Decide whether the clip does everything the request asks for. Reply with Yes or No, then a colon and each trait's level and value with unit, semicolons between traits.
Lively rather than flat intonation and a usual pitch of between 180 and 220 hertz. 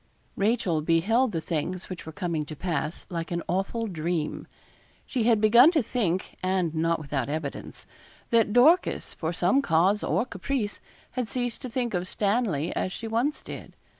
Yes: wide, 5.9 semitones; high, 190 Hz